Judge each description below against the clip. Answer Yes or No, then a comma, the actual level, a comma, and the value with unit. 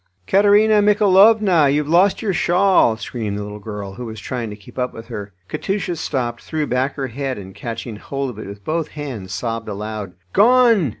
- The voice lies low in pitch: Yes, low, 130 Hz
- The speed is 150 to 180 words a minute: No, average, 190 wpm